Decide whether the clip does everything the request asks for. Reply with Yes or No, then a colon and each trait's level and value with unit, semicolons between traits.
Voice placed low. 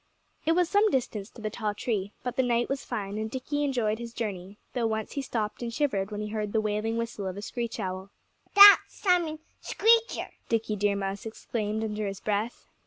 No: high, 220 Hz